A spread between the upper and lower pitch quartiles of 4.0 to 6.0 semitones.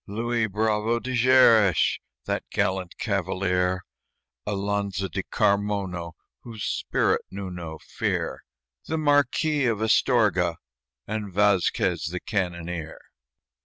No: average, 3.6 semitones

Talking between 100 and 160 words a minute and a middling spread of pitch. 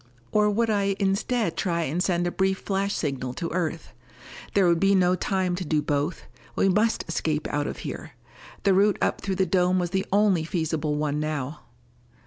No: average, 190 wpm; average, 3.7 semitones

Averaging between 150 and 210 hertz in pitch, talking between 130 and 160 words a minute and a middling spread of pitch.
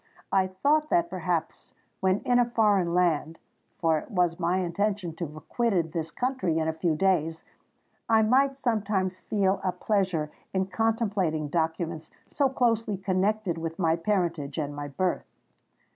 Yes: medium, 185 Hz; average, 145 wpm; average, 4.7 semitones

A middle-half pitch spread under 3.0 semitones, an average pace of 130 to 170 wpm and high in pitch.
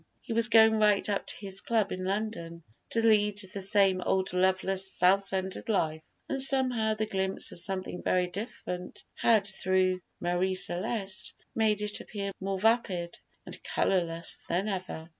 Yes: narrow, 2.6 semitones; average, 165 wpm; high, 195 Hz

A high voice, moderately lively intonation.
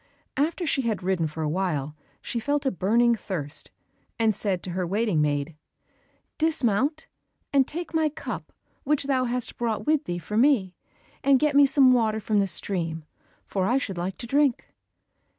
No: high, 225 Hz; wide, 7.2 semitones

